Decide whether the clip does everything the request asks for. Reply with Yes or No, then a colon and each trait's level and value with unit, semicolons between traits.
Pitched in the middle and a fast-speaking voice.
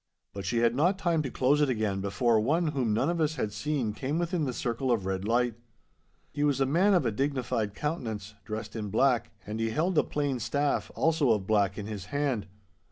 No: low, 125 Hz; fast, 220 wpm